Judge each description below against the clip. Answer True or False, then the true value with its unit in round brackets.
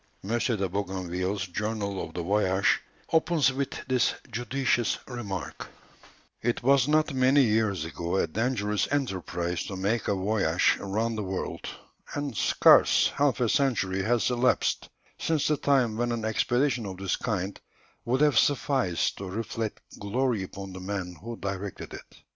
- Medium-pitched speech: False (110 Hz)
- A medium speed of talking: True (150 wpm)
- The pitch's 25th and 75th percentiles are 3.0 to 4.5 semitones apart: False (4.9 semitones)